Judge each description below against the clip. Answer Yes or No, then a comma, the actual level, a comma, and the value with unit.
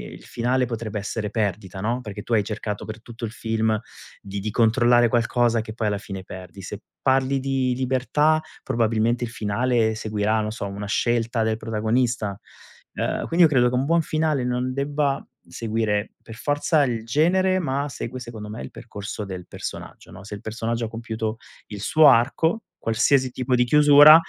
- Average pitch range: Yes, average, 3.2 semitones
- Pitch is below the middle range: Yes, low, 115 Hz